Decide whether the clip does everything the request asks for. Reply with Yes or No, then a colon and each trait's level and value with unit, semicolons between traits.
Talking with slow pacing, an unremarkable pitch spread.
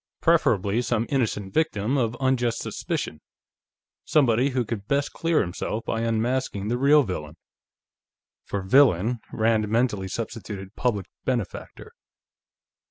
Yes: slow, 115 wpm; average, 3.9 semitones